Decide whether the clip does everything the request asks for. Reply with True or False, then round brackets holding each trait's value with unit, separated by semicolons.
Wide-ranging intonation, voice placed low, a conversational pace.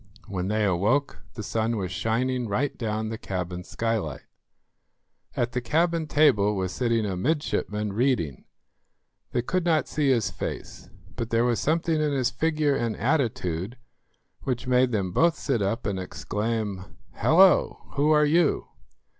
True (5.9 semitones; 115 Hz; 150 wpm)